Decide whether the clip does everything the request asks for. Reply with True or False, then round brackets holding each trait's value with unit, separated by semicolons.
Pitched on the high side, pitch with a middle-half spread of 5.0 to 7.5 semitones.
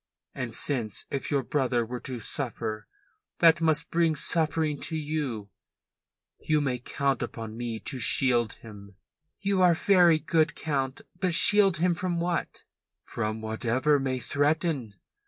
False (140 Hz; 5.5 semitones)